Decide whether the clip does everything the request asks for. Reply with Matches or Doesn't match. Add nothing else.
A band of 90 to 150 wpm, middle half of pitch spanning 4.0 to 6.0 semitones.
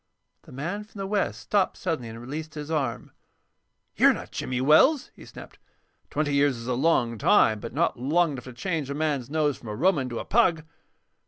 Doesn't match